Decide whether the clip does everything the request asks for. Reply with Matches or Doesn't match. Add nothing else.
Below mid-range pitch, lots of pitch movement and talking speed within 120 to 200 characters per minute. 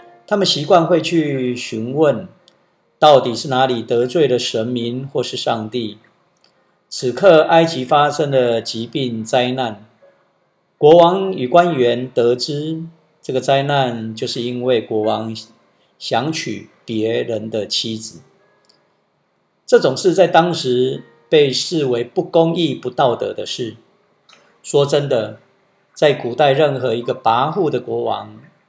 Matches